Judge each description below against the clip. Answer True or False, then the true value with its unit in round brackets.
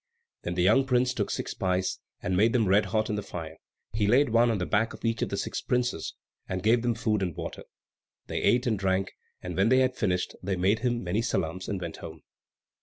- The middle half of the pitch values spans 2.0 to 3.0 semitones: False (4.3 semitones)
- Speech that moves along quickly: True (240 wpm)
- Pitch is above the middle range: False (105 Hz)